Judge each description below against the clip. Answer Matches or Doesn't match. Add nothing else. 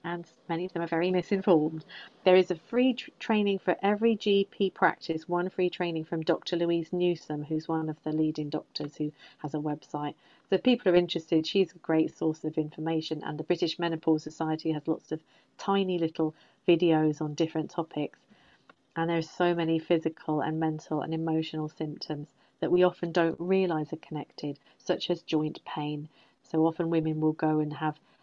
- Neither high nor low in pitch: Matches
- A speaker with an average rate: Matches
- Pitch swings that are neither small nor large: Doesn't match